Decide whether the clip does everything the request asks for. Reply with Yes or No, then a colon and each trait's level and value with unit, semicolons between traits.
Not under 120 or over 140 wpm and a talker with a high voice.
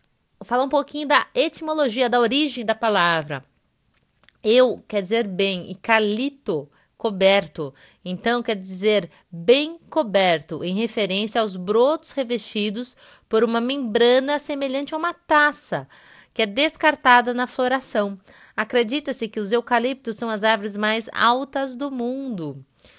Yes: average, 130 wpm; high, 230 Hz